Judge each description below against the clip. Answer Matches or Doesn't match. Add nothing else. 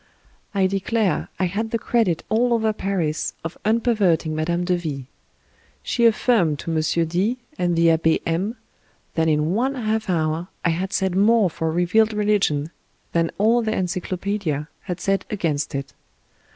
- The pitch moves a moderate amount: Matches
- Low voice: Doesn't match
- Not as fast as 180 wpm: Matches